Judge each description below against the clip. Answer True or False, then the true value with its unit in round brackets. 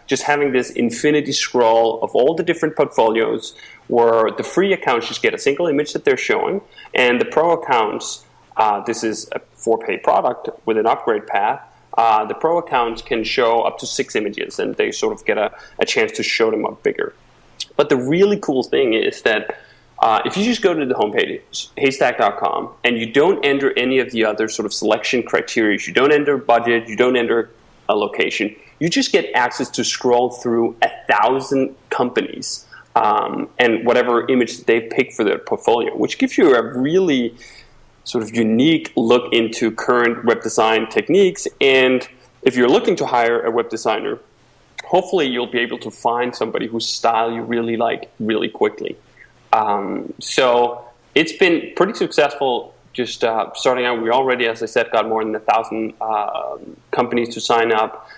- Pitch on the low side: True (125 Hz)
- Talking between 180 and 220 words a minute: True (185 wpm)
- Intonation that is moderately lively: False (6.9 semitones)